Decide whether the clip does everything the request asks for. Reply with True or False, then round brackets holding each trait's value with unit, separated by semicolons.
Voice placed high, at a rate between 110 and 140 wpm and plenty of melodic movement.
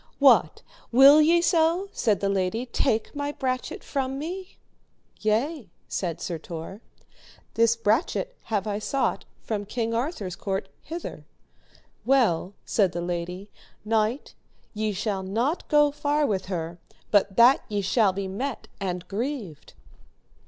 True (220 Hz; 135 wpm; 6.2 semitones)